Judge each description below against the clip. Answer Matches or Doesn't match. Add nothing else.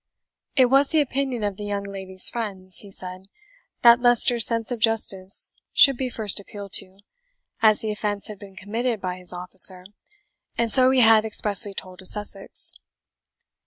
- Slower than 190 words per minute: Matches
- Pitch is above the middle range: Matches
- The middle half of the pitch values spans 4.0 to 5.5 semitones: Doesn't match